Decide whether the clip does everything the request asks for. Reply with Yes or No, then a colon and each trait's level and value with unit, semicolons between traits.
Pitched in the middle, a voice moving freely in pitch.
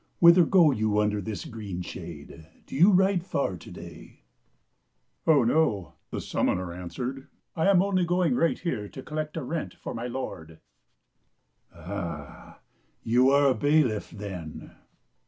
No: low, 125 Hz; wide, 8.1 semitones